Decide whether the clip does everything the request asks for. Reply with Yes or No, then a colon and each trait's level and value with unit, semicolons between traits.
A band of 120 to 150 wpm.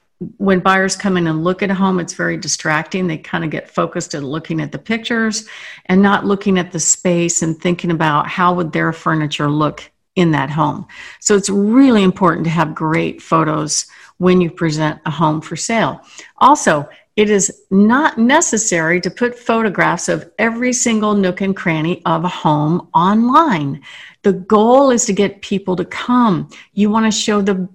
No: average, 185 wpm